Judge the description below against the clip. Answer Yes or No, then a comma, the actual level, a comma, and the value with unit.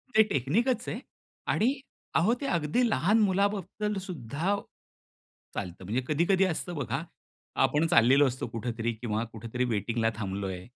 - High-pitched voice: No, medium, 145 Hz